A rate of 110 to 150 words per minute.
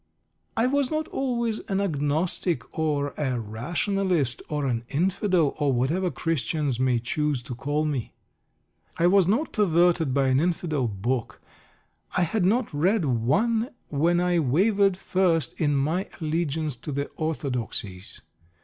Yes: average, 140 wpm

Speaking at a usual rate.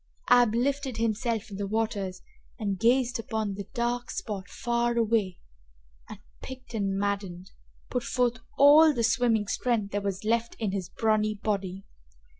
Yes: average, 150 wpm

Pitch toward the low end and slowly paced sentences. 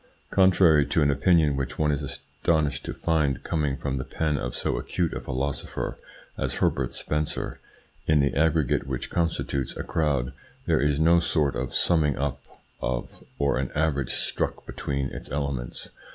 No: very low, 70 Hz; average, 165 wpm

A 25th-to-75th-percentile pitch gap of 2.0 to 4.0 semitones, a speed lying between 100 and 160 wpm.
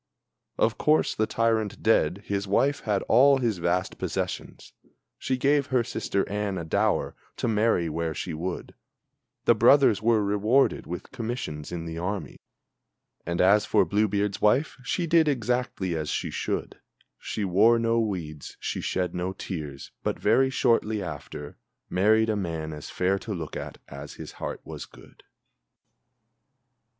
No: average, 4.9 semitones; average, 155 wpm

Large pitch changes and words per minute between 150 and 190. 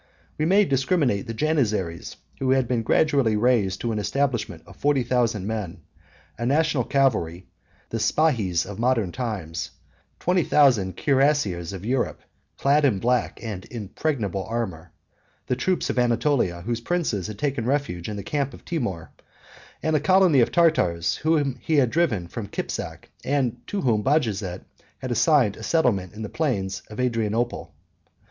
Yes: wide, 5.7 semitones; average, 155 wpm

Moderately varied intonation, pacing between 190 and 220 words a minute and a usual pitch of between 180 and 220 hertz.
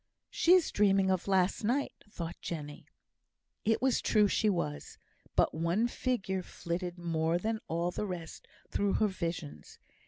No: average, 3.9 semitones; average, 150 wpm; medium, 185 Hz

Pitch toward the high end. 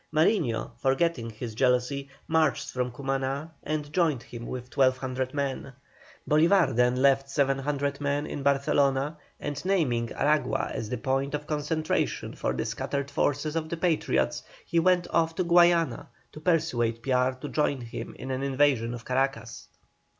No: medium, 140 Hz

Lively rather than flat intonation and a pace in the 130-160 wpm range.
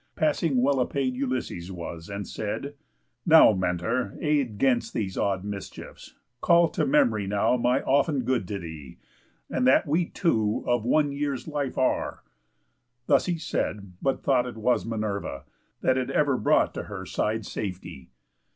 Yes: wide, 5.8 semitones; average, 155 wpm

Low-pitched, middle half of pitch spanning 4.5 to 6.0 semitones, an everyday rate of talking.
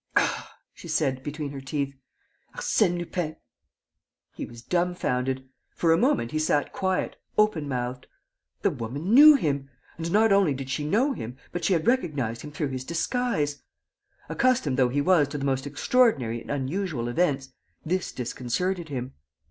No: medium, 150 Hz; wide, 5.4 semitones; average, 160 wpm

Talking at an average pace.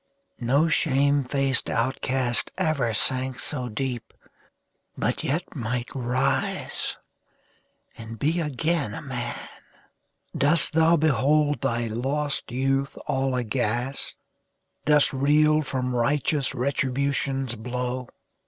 No: slow, 100 wpm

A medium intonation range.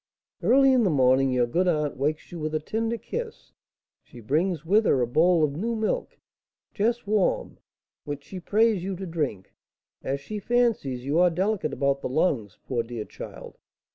No: wide, 7.4 semitones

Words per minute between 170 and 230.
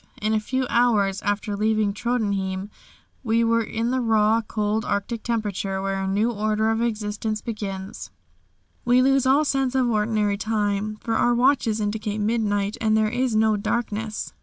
No: average, 160 wpm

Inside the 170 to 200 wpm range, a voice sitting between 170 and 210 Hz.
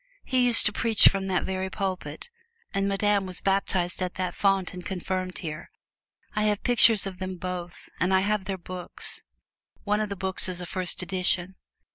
Yes: average, 185 wpm; high, 190 Hz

